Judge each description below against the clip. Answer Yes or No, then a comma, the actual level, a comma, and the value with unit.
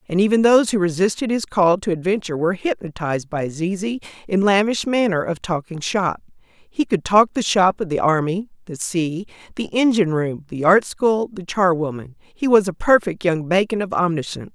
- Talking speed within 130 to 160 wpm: No, average, 190 wpm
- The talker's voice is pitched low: No, medium, 185 Hz